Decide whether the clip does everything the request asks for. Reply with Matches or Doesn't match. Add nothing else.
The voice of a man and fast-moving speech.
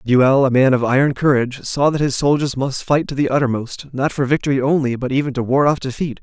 Matches